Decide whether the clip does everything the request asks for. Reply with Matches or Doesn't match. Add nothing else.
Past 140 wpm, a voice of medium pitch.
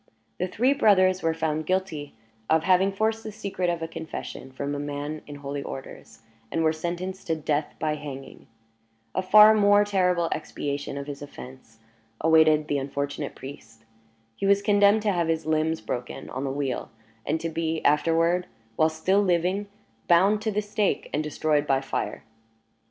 Matches